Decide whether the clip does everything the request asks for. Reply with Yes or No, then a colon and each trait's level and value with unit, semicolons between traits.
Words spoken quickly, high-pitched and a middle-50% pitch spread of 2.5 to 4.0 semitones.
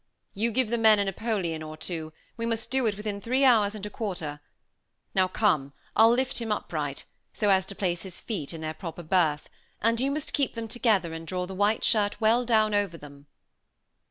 No: fast, 210 wpm; high, 205 Hz; average, 5.0 semitones